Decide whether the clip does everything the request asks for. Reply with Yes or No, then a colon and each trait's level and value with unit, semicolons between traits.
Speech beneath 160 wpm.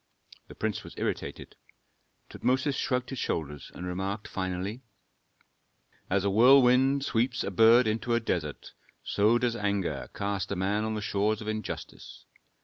Yes: average, 145 wpm